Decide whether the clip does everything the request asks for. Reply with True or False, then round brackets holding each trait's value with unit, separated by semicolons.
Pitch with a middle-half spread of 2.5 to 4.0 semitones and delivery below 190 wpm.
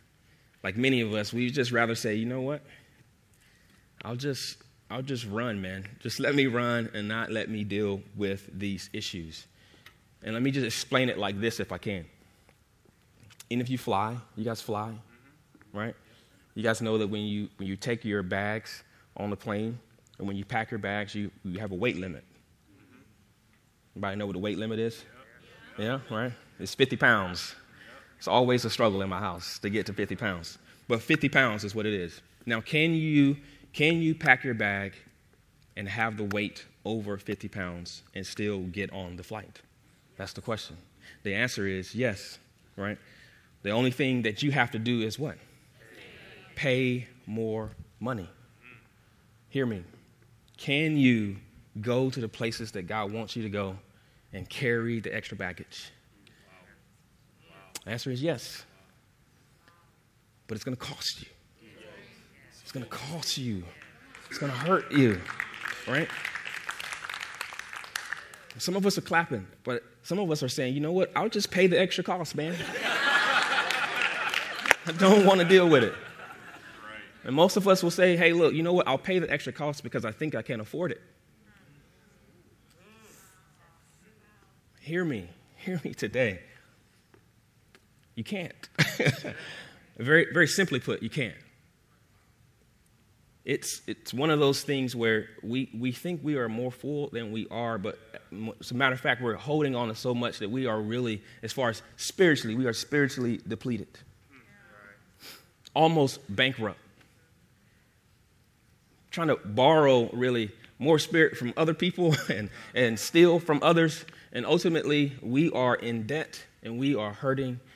False (4.7 semitones; 160 wpm)